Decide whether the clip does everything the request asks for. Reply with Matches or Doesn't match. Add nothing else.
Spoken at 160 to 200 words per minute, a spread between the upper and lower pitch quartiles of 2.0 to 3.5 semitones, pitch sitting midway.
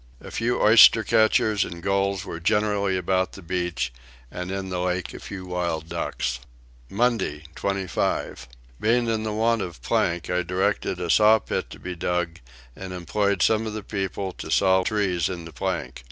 Doesn't match